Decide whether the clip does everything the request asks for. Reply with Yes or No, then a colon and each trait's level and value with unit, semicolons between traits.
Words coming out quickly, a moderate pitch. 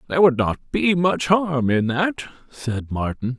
No: average, 175 wpm; medium, 145 Hz